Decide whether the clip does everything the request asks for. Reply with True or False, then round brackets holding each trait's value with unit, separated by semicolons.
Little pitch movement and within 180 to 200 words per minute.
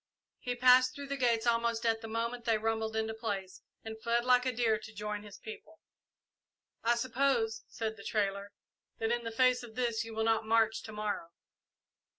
True (1.5 semitones; 190 wpm)